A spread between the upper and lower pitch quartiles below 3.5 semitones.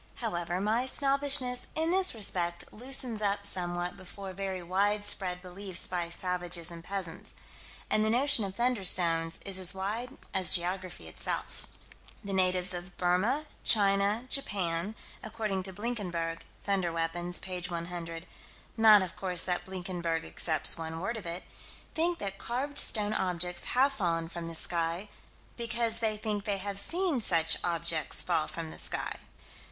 No: average, 3.8 semitones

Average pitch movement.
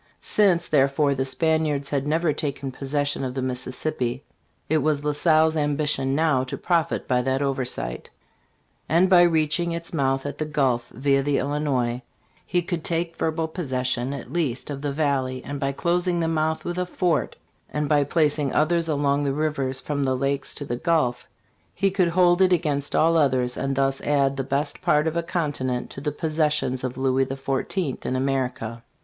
Yes: average, 3.1 semitones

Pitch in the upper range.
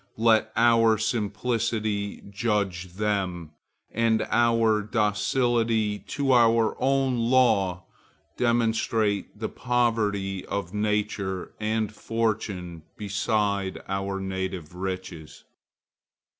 No: low, 105 Hz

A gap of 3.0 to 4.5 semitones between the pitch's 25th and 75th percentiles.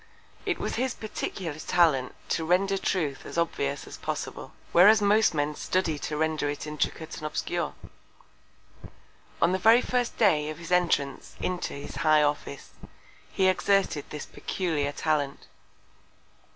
Yes: average, 4.2 semitones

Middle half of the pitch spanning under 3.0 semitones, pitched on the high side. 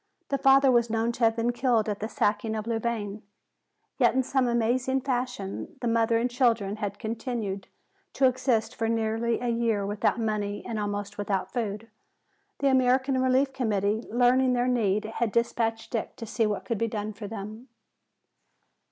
Yes: narrow, 2.6 semitones; high, 230 Hz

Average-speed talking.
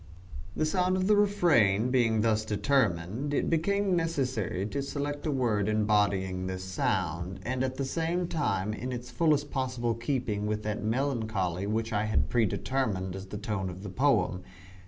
Yes: average, 170 wpm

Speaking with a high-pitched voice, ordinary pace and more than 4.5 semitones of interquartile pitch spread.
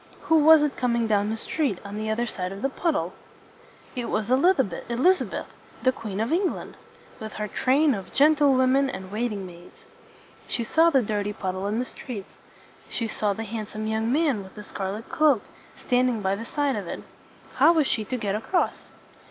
No: high, 230 Hz; fast, 210 wpm; average, 4.9 semitones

